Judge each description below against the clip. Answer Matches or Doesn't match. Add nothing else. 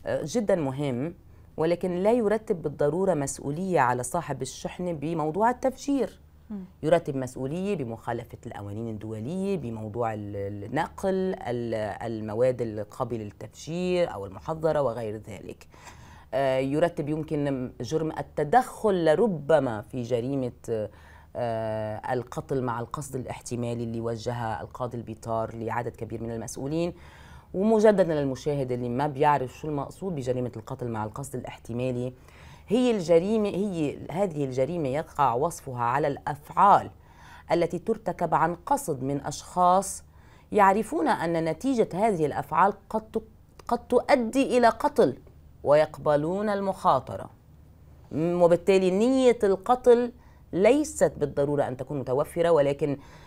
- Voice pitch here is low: Doesn't match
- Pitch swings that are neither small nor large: Doesn't match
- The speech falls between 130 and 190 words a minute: Doesn't match